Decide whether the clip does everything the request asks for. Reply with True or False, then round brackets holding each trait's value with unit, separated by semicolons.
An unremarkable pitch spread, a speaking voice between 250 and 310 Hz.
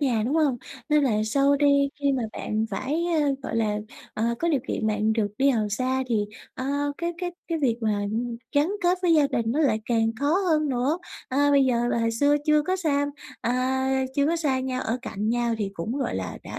True (4.3 semitones; 265 Hz)